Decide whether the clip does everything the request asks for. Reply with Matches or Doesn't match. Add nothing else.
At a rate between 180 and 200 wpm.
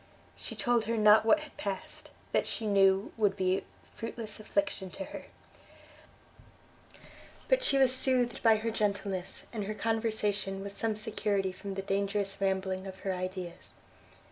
Doesn't match